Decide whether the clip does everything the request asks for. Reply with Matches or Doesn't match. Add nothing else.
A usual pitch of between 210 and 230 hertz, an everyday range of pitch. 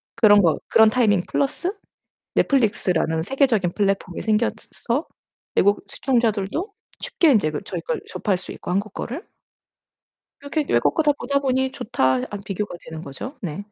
Doesn't match